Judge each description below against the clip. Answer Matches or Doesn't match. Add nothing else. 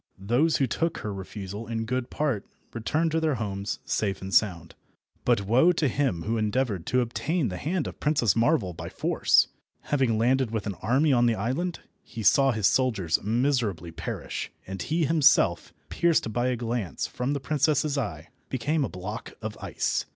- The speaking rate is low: Doesn't match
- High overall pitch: Doesn't match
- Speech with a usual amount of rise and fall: Doesn't match